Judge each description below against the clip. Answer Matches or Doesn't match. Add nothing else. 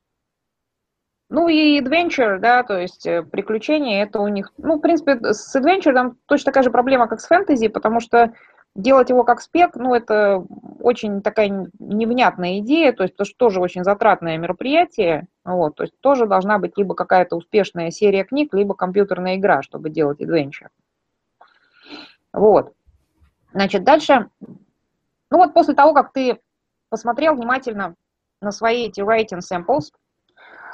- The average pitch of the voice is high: Matches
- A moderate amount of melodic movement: Doesn't match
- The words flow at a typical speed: Matches